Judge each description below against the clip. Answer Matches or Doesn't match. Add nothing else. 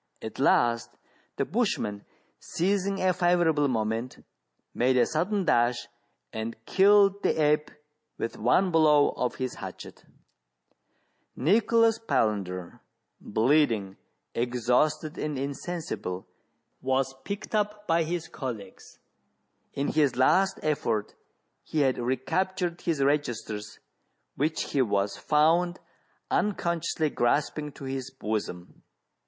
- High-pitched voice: Doesn't match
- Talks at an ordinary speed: Doesn't match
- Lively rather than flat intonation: Matches